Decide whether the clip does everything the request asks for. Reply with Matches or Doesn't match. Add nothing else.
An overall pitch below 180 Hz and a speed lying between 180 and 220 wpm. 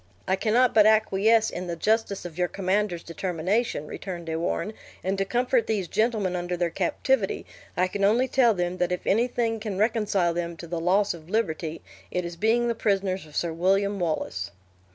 Doesn't match